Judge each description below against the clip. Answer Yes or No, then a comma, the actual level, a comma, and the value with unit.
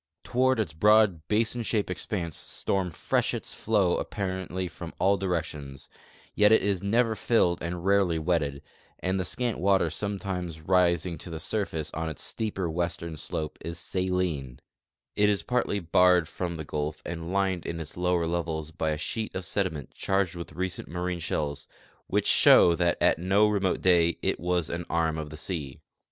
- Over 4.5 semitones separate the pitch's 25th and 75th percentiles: No, average, 3.1 semitones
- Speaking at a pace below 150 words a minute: No, average, 170 wpm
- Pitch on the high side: No, very low, 90 Hz